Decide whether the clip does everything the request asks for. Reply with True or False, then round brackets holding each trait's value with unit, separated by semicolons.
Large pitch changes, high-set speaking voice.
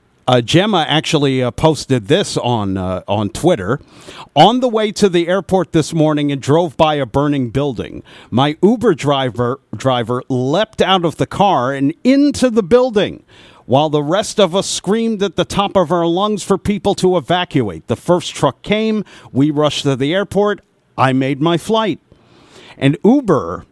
False (6.5 semitones; 160 Hz)